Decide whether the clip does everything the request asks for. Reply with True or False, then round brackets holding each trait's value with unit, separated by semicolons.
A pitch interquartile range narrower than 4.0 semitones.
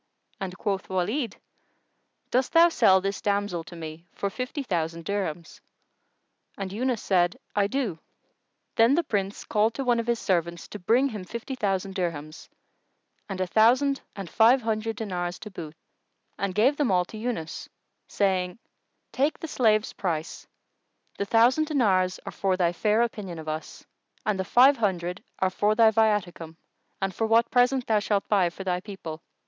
False (4.3 semitones)